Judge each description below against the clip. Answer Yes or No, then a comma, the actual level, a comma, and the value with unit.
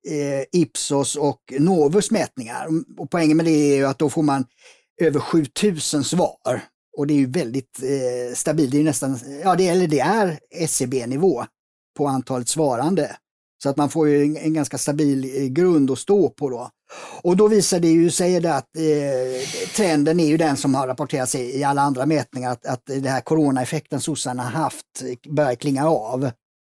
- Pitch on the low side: No, medium, 145 Hz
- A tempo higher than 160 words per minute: Yes, average, 175 wpm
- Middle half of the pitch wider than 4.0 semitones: No, average, 3.1 semitones